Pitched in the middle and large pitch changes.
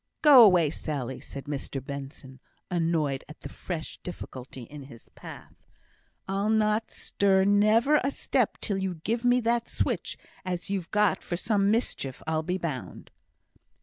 Yes: medium, 180 Hz; wide, 6.5 semitones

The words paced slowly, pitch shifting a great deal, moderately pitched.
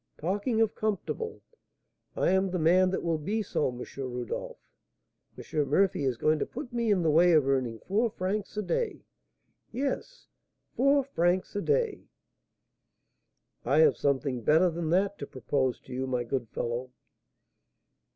No: average, 155 wpm; wide, 7.7 semitones; medium, 175 Hz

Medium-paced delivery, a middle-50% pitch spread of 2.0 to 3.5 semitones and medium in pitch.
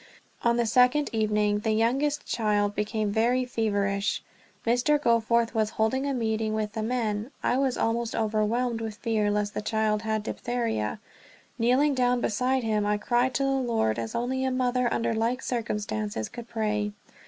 No: average, 165 wpm; average, 2.7 semitones; high, 225 Hz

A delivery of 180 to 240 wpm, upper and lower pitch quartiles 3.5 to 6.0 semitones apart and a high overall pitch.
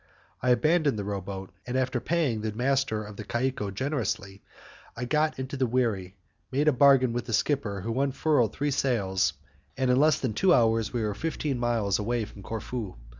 No: average, 190 wpm; average, 4.5 semitones; low, 120 Hz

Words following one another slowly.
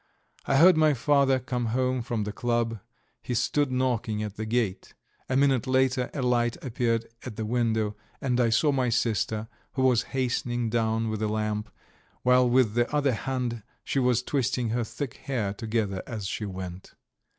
No: average, 175 wpm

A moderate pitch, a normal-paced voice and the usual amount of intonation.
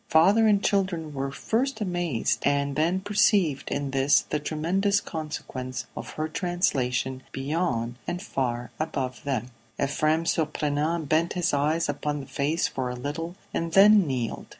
Yes: medium, 155 Hz; average, 150 wpm; average, 4.3 semitones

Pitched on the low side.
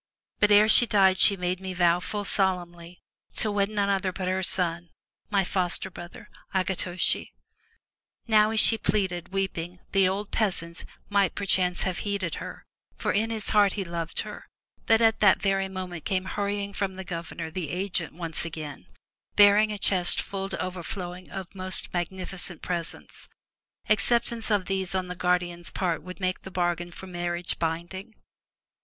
No: medium, 185 Hz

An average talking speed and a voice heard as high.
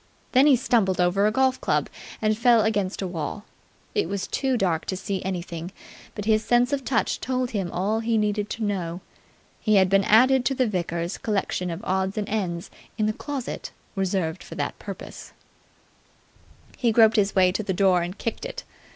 Yes: average, 190 wpm; high, 205 Hz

